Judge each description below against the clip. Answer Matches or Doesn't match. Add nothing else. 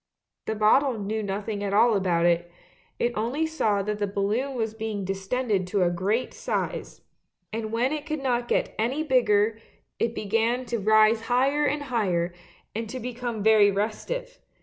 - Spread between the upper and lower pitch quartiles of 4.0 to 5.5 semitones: Doesn't match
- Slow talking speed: Doesn't match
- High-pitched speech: Matches